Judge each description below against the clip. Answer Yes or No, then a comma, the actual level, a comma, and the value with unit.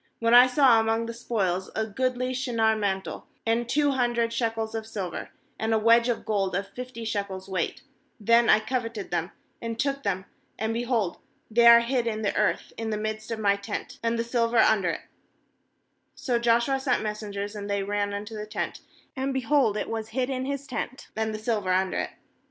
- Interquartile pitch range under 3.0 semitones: Yes, narrow, 2.5 semitones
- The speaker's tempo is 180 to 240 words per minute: Yes, average, 200 wpm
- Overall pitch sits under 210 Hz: No, high, 225 Hz